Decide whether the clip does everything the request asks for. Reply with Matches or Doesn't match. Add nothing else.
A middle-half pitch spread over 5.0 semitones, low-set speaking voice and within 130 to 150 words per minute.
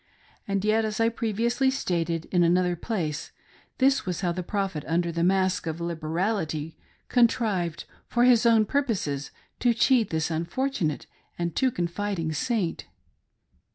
Doesn't match